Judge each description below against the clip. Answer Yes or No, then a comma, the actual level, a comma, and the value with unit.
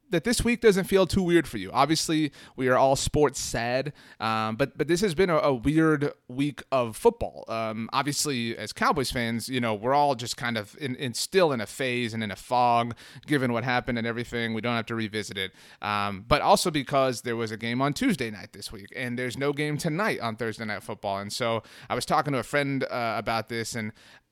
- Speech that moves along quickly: Yes, fast, 230 wpm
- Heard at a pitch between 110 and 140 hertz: Yes, low, 125 Hz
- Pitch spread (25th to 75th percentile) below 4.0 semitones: No, average, 4.3 semitones